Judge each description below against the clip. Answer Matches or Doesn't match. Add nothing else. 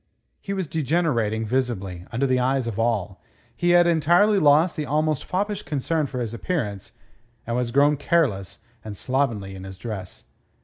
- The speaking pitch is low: Matches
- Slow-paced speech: Doesn't match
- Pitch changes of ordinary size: Doesn't match